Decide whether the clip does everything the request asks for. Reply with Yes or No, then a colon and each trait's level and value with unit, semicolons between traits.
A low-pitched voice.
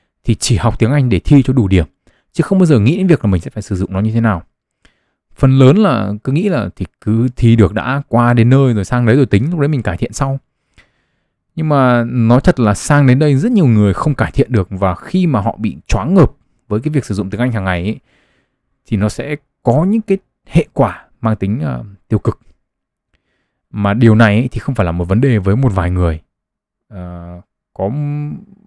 Yes: low, 115 Hz